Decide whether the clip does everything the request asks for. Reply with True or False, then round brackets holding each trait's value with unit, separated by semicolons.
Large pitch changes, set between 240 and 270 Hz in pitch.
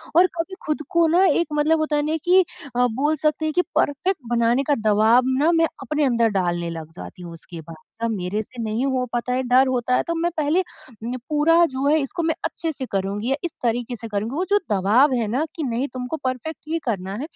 True (5.7 semitones; 260 Hz)